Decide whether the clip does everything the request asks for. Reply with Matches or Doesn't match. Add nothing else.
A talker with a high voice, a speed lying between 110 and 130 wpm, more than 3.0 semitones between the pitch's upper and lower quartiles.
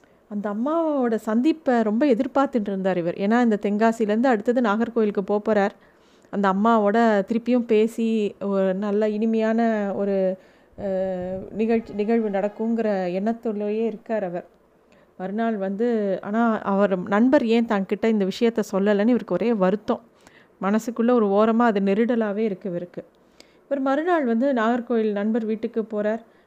Doesn't match